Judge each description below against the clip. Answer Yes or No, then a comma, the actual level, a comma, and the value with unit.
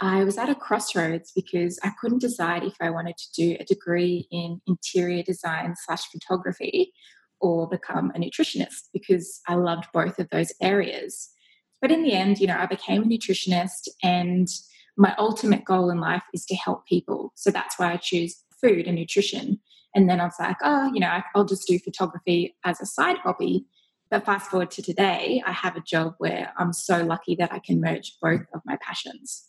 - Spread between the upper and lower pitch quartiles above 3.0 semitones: No, narrow, 2.4 semitones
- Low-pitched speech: No, medium, 185 Hz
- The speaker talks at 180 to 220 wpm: Yes, average, 195 wpm